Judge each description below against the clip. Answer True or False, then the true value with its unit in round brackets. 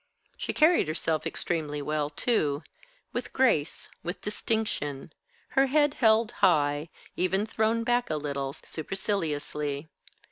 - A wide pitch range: True (7.1 semitones)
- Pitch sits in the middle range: True (165 Hz)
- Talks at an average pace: False (115 wpm)